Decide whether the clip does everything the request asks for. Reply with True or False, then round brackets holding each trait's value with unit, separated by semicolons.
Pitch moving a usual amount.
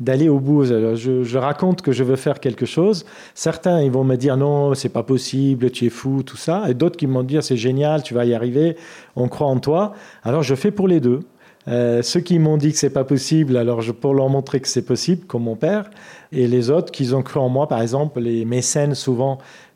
True (3.7 semitones)